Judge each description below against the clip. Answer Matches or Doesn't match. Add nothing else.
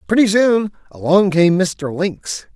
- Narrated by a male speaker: Matches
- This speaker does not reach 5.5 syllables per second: Matches